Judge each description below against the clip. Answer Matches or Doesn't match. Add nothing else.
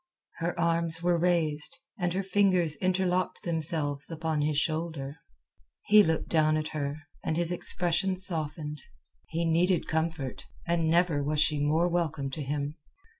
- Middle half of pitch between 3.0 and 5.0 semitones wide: Doesn't match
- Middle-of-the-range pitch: Matches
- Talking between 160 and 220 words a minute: Doesn't match